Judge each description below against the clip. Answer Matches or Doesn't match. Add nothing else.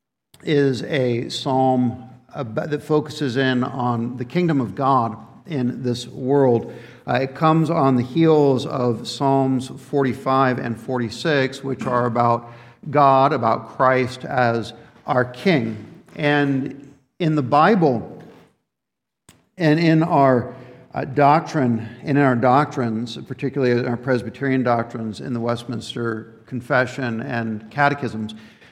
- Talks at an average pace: Doesn't match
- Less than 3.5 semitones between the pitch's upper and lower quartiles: Matches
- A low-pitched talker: Matches